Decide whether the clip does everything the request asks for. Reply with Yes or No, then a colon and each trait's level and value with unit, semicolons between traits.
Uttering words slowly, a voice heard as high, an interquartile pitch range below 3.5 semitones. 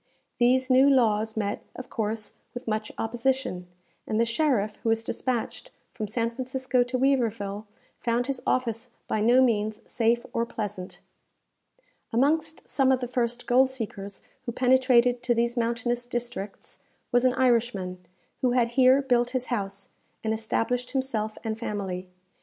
No: average, 150 wpm; high, 240 Hz; average, 2.7 semitones